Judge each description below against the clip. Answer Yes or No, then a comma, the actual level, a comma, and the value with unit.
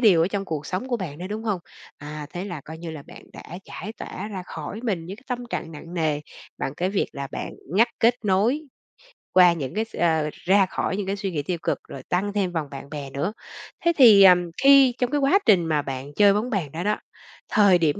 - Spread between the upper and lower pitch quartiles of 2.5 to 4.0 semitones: No, average, 4.9 semitones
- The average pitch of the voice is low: No, medium, 185 Hz